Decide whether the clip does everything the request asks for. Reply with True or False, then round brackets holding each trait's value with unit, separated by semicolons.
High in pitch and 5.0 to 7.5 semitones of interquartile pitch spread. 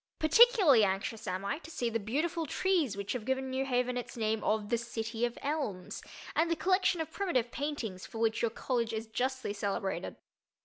True (240 Hz; 5.3 semitones)